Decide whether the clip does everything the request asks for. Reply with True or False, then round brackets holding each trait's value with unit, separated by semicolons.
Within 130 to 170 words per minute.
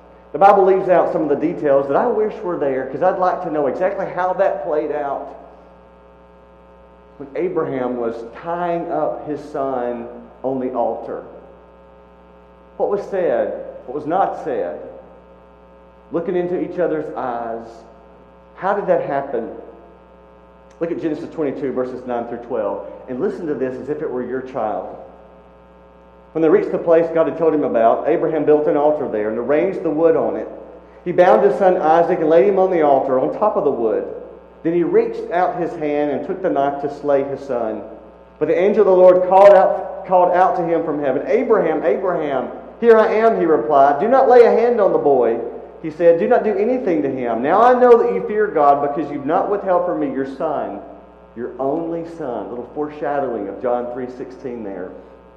False (195 wpm)